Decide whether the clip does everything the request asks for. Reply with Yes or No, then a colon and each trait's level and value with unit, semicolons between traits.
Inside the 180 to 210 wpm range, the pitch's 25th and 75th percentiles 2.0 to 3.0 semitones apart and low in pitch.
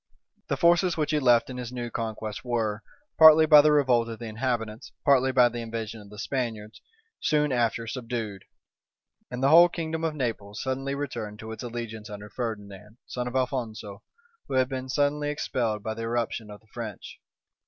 No: average, 185 wpm; average, 3.5 semitones; low, 120 Hz